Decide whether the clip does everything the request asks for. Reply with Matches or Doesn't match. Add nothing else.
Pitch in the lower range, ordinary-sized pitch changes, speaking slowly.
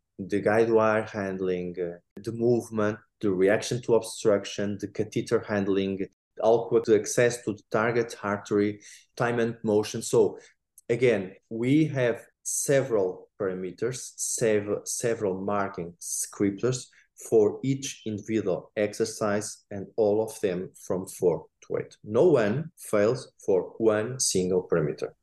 Matches